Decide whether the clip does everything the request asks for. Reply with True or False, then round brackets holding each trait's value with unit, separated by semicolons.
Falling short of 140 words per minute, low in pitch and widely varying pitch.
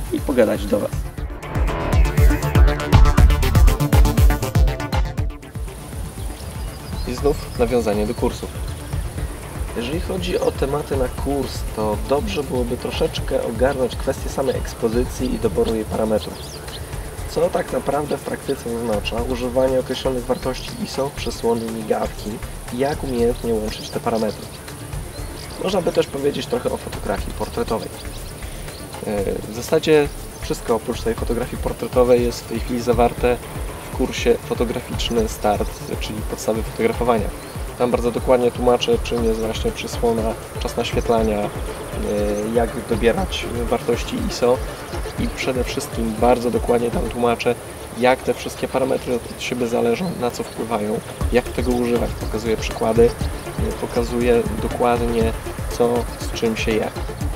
False (120 wpm; 115 Hz; 2.7 semitones)